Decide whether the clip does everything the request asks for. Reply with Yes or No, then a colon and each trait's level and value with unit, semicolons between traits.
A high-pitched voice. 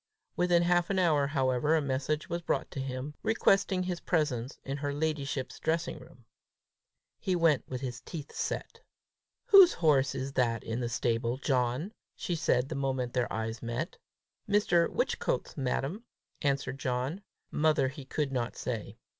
No: medium, 140 Hz